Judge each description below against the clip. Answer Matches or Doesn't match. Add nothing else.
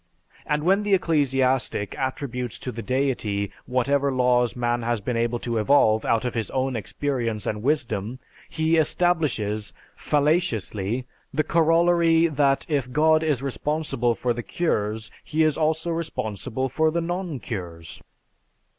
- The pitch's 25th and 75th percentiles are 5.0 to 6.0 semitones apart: Matches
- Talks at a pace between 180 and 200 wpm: Doesn't match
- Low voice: Matches